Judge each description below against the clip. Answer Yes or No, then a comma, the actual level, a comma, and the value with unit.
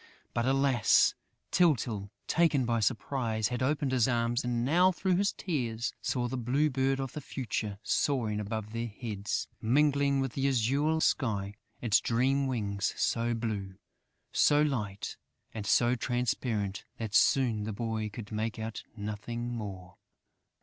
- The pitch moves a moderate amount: Yes, average, 3.8 semitones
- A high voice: No, low, 120 Hz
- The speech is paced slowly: No, average, 145 wpm